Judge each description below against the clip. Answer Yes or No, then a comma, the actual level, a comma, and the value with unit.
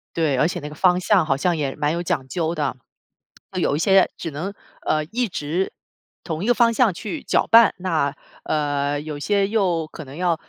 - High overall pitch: No, medium, 165 Hz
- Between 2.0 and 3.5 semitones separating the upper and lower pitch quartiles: No, average, 4.3 semitones